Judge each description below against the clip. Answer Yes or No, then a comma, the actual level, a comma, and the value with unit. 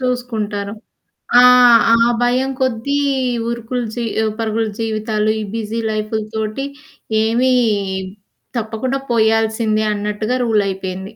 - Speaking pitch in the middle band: No, high, 220 Hz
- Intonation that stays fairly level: Yes, narrow, 1.9 semitones